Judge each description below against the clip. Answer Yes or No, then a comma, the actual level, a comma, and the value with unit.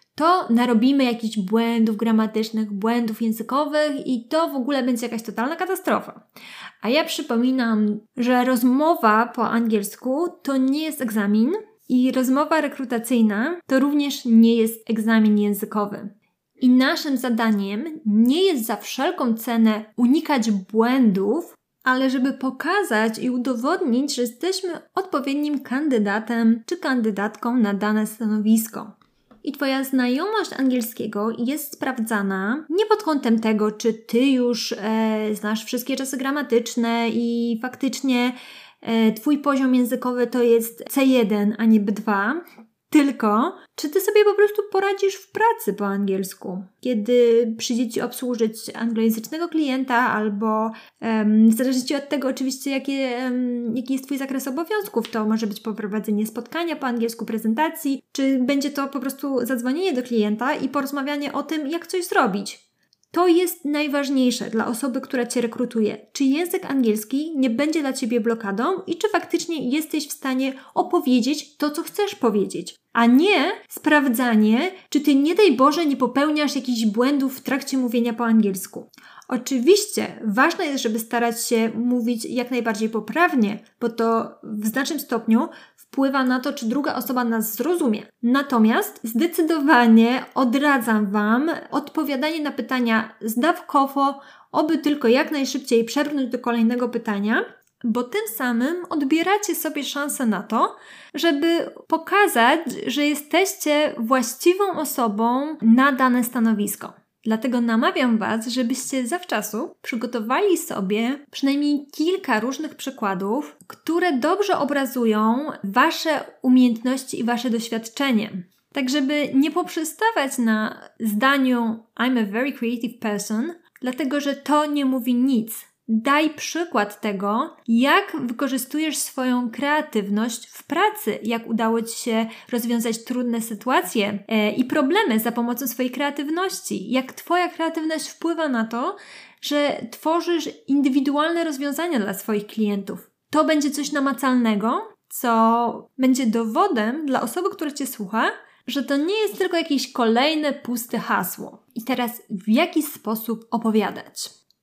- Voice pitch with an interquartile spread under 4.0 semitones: No, average, 4.5 semitones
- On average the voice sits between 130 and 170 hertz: No, very high, 255 Hz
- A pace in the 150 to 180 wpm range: No, average, 130 wpm